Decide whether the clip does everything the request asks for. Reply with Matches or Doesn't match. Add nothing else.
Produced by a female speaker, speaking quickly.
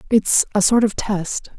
Doesn't match